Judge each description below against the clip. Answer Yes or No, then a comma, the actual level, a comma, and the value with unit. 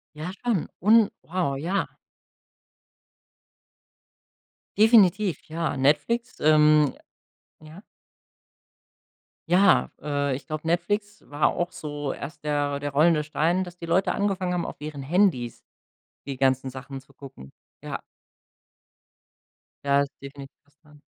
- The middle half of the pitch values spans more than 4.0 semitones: Yes, average, 4.4 semitones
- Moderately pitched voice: Yes, medium, 155 Hz